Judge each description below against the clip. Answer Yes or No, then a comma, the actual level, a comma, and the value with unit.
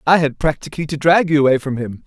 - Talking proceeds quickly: Yes, fast, 260 wpm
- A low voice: No, medium, 150 Hz